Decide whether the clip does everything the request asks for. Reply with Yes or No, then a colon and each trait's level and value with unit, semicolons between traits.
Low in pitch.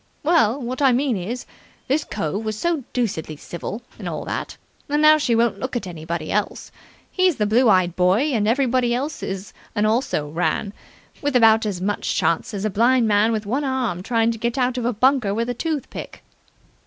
No: high, 230 Hz